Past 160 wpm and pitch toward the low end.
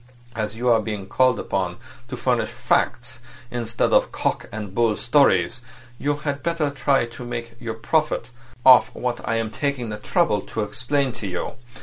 Yes: average, 175 wpm; low, 120 Hz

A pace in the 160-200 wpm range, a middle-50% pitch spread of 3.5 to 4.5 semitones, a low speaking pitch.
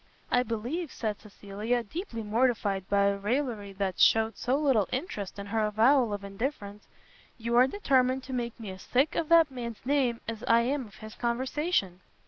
No: average, 180 wpm; average, 4.0 semitones; high, 235 Hz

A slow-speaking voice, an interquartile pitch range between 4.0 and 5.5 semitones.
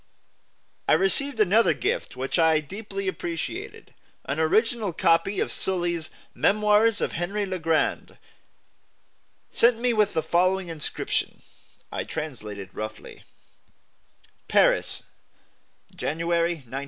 Yes: slow, 110 wpm; average, 4.6 semitones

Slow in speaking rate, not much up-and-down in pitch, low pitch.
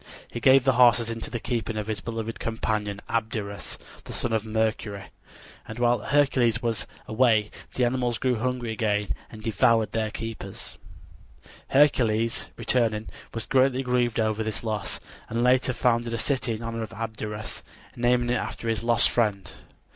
No: average, 160 wpm; narrow, 1.9 semitones; low, 115 Hz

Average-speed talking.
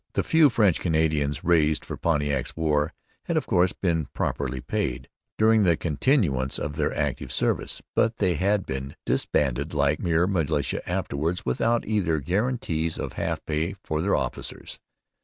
Yes: average, 155 wpm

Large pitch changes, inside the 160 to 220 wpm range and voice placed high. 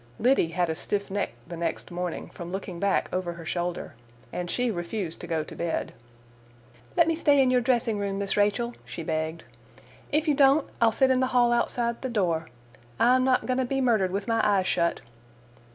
Yes: wide, 6.4 semitones; average, 200 wpm; high, 205 Hz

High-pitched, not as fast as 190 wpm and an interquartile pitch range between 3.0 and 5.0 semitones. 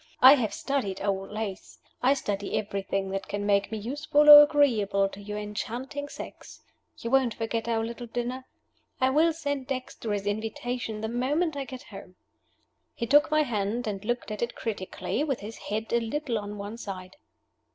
Yes: high, 230 Hz; average, 180 wpm; average, 4.4 semitones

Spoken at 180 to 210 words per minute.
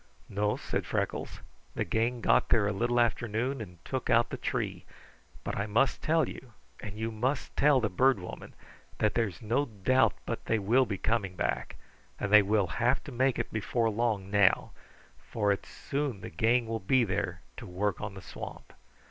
Yes: average, 190 wpm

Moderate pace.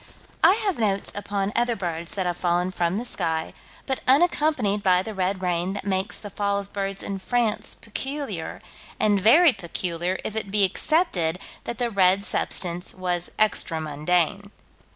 Yes: average, 165 wpm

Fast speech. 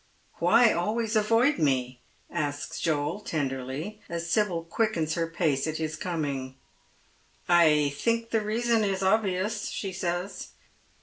No: average, 140 wpm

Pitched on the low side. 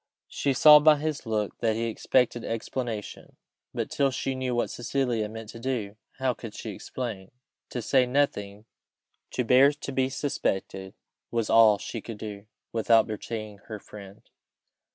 Yes: low, 115 Hz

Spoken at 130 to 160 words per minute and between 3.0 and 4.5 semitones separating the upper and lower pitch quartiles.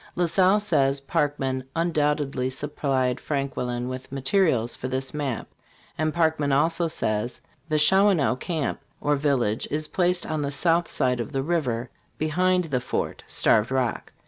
Yes: average, 145 wpm; average, 4.1 semitones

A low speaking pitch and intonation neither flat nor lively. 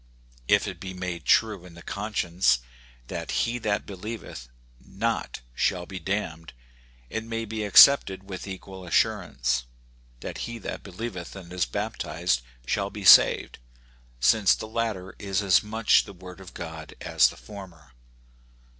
Yes: very low, 95 Hz; average, 3.4 semitones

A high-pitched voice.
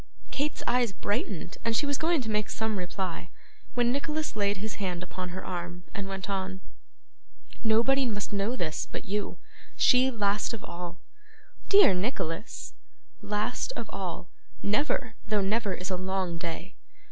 Yes: high, 205 Hz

